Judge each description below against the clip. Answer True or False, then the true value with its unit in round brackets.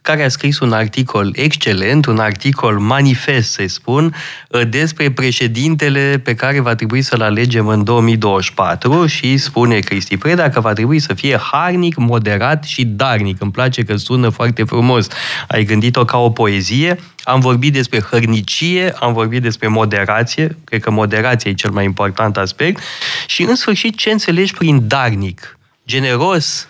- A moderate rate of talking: True (155 wpm)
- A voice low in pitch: True (120 Hz)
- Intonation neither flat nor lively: True (4.6 semitones)